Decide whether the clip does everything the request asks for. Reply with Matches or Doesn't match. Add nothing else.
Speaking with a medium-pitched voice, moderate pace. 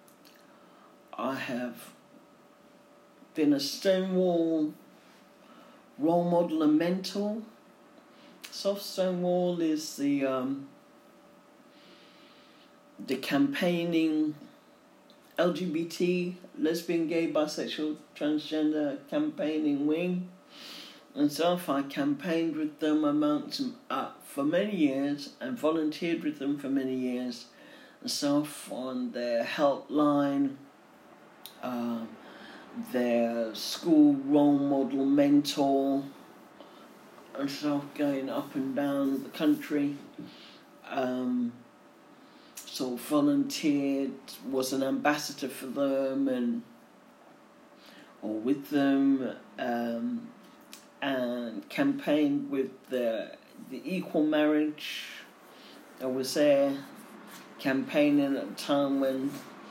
Doesn't match